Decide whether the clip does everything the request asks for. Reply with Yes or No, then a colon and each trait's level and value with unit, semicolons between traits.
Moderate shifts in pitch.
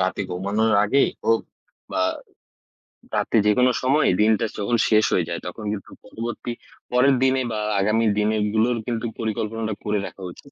No: narrow, 2.3 semitones